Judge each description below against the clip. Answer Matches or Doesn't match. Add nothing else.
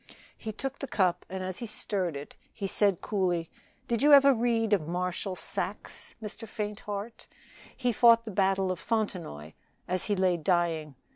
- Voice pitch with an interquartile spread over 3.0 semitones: Matches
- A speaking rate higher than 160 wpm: Matches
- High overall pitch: Matches